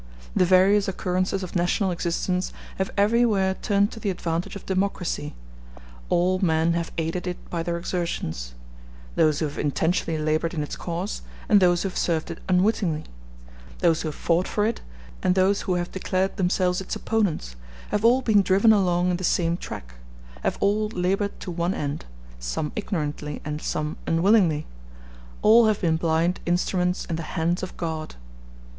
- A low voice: No, medium, 180 Hz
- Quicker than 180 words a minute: No, average, 170 wpm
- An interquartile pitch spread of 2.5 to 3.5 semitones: Yes, average, 2.9 semitones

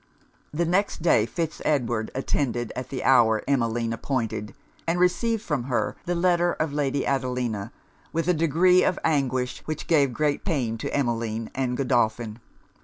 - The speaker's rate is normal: Yes, average, 155 wpm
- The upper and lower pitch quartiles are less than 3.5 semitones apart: No, wide, 5.6 semitones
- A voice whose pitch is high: No, low, 135 Hz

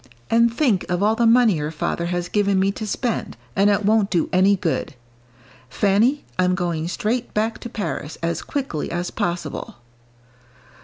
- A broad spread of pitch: No, average, 4.3 semitones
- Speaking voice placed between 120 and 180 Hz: No, high, 200 Hz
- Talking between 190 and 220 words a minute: No, average, 165 wpm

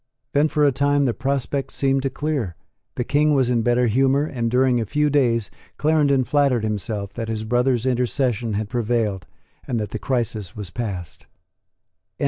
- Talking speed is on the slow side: No, average, 170 wpm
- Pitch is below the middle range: Yes, low, 125 Hz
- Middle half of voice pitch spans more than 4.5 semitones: No, average, 3.9 semitones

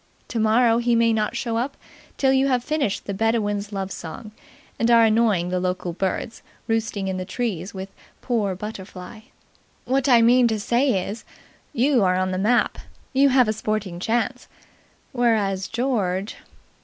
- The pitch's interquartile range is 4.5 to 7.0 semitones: No, average, 3.8 semitones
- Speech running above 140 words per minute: Yes, average, 160 wpm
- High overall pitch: Yes, high, 220 Hz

